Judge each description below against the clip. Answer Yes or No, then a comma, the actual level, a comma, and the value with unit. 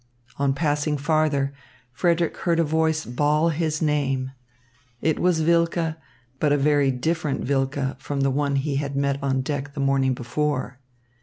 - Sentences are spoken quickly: No, average, 155 wpm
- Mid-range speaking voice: Yes, medium, 145 Hz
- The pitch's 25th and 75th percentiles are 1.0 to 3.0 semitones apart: Yes, narrow, 2.4 semitones